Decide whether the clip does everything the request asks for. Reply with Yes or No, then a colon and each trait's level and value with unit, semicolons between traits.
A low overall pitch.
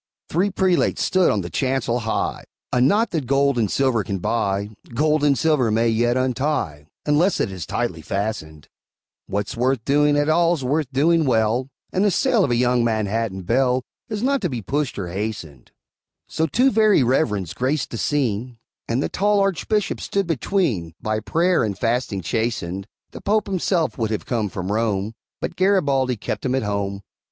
Yes: low, 125 Hz